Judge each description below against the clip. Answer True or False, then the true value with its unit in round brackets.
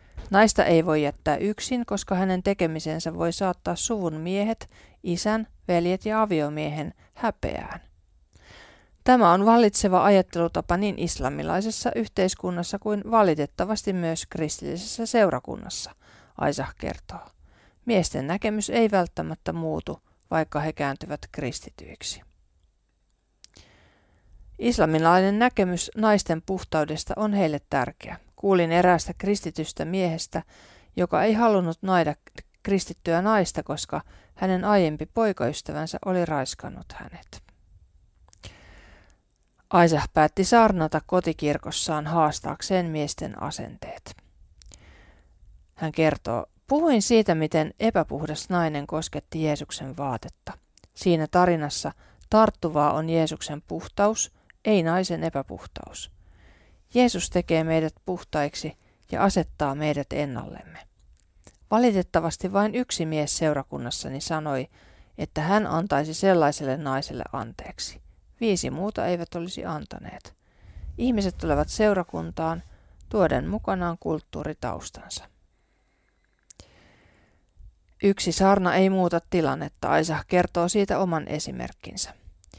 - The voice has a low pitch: False (165 Hz)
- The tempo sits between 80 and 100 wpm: True (95 wpm)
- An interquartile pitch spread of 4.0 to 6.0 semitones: True (5.4 semitones)